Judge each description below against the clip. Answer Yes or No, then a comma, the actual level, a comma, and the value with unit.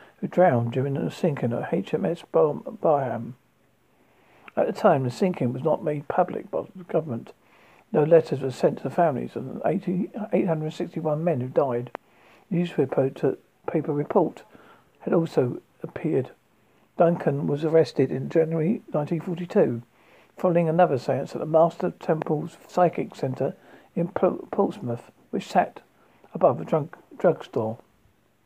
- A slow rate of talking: Yes, slow, 130 wpm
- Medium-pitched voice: Yes, medium, 160 Hz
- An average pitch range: Yes, average, 4.2 semitones